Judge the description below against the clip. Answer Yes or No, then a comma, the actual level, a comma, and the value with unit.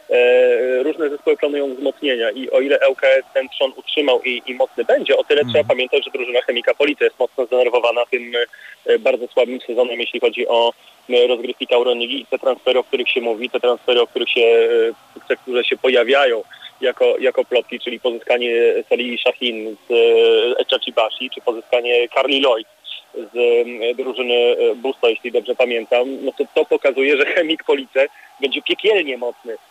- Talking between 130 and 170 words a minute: Yes, fast, 160 wpm